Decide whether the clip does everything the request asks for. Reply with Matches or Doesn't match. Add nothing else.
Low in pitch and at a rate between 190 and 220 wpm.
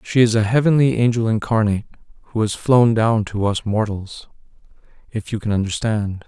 Doesn't match